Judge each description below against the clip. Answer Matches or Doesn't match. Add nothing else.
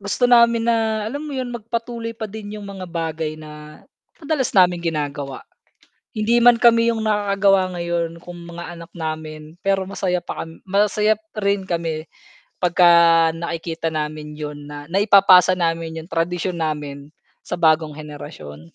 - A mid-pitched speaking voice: Matches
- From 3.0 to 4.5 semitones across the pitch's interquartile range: Doesn't match